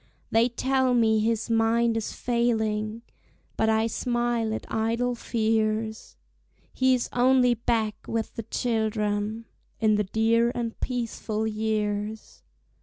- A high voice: Yes, high, 225 Hz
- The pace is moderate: No, slow, 120 wpm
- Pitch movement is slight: Yes, narrow, 1.5 semitones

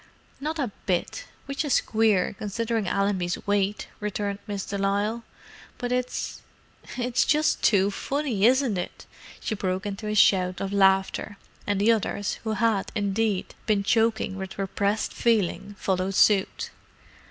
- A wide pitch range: No, average, 2.7 semitones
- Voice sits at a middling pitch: No, high, 205 Hz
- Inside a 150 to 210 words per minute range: No, average, 140 wpm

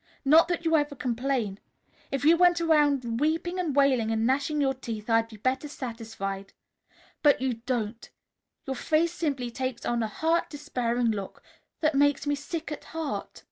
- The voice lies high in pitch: Yes, very high, 270 Hz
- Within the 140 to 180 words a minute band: Yes, average, 170 wpm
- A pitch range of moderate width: Yes, average, 4.8 semitones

